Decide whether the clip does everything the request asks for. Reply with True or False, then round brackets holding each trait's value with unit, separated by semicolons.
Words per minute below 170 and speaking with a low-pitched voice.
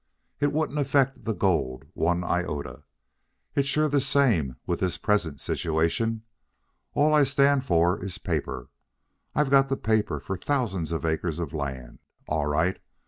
True (150 wpm; 95 Hz)